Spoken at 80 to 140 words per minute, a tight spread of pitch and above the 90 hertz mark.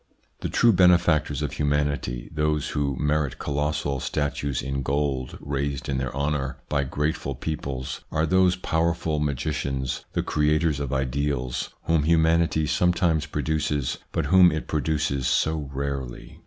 No: slow, 135 wpm; narrow, 2.3 semitones; very low, 75 Hz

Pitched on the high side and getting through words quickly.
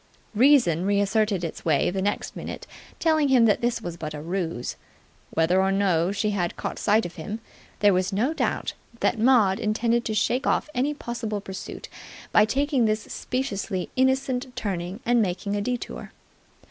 No: high, 210 Hz; average, 170 wpm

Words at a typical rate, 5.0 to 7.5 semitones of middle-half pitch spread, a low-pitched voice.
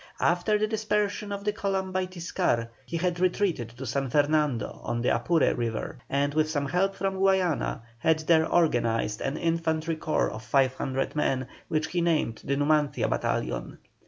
No: average, 165 wpm; wide, 5.4 semitones; medium, 160 Hz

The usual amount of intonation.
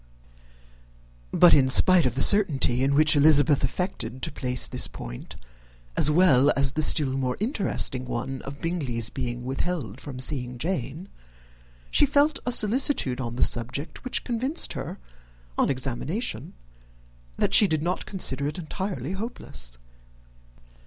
No: wide, 6.3 semitones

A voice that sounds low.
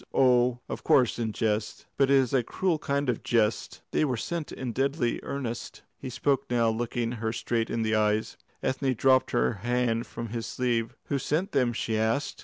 Yes: low, 120 Hz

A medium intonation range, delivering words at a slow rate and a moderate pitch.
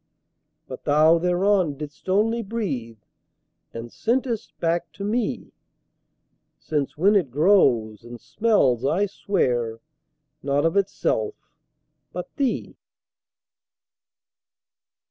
No: wide, 7.3 semitones; slow, 95 wpm; medium, 170 Hz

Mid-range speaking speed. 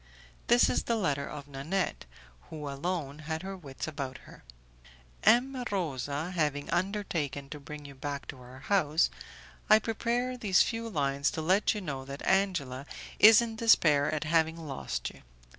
Yes: average, 160 wpm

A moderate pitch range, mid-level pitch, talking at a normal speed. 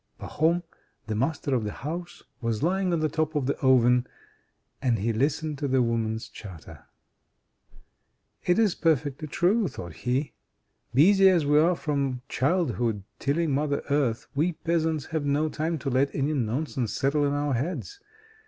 Yes: average, 4.3 semitones; medium, 145 Hz; average, 160 wpm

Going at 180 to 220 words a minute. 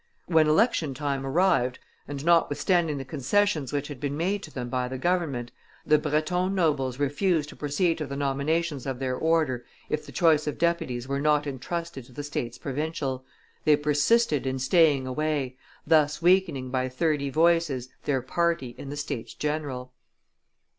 No: average, 165 wpm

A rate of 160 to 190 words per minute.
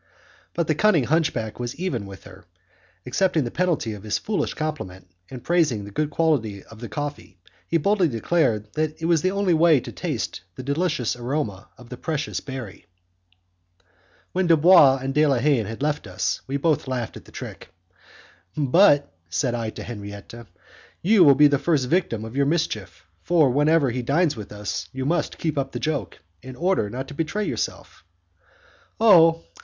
Yes: average, 180 wpm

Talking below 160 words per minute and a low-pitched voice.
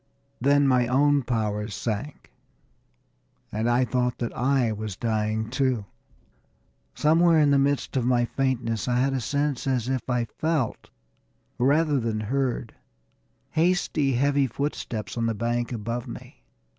Yes: average, 140 wpm; low, 125 Hz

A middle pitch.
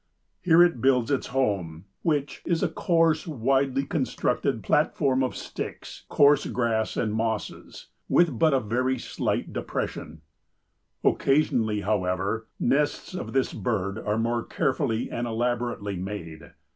No: low, 120 Hz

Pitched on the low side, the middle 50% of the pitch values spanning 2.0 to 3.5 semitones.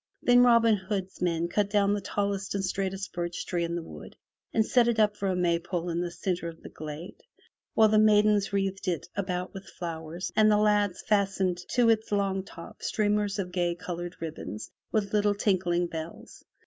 No: high, 195 Hz; average, 3.0 semitones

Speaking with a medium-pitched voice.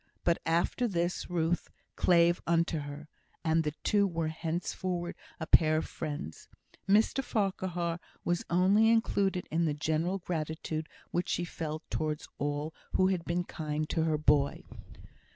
Yes: medium, 170 Hz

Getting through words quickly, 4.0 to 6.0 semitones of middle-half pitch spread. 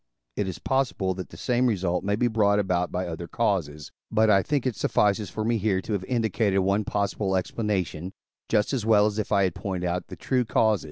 No: fast, 220 wpm; average, 2.9 semitones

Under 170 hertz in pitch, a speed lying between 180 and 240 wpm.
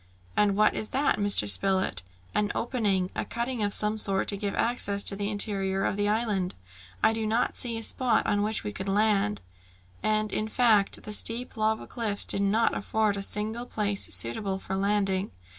No: high, 210 Hz; average, 190 wpm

